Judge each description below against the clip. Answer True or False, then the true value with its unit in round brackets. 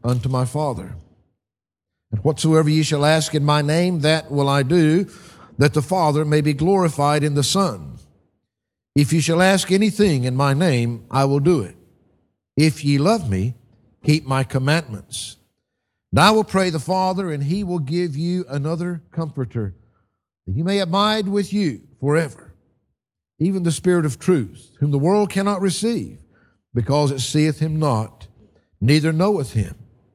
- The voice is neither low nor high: True (150 Hz)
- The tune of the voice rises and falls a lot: True (6.6 semitones)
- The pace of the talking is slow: False (160 wpm)